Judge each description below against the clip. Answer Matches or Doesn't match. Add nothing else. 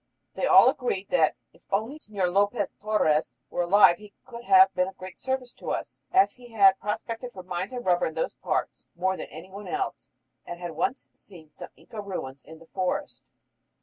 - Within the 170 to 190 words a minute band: Doesn't match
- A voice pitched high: Matches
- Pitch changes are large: Doesn't match